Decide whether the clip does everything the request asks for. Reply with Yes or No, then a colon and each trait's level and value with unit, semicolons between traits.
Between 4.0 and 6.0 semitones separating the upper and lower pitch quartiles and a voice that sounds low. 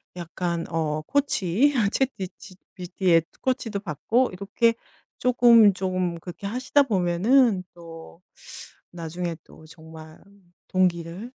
No: average, 5.2 semitones; medium, 185 Hz